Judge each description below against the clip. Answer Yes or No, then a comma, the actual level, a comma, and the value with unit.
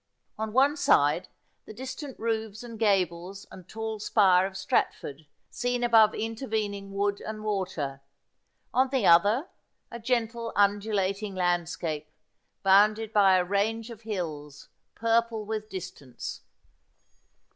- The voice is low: No, high, 210 Hz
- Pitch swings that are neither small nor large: Yes, average, 3.3 semitones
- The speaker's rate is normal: No, slow, 125 wpm